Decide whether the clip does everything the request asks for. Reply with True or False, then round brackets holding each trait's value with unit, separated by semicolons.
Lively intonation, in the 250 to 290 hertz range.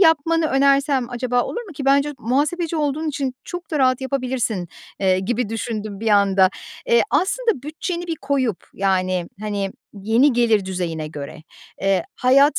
True (6.5 semitones; 255 Hz)